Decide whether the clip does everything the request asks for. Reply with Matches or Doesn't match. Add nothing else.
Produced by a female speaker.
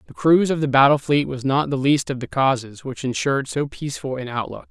Doesn't match